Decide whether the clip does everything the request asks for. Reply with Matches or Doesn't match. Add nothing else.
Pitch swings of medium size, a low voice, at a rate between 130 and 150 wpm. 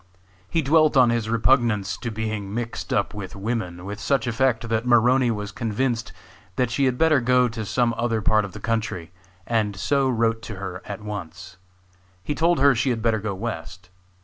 Doesn't match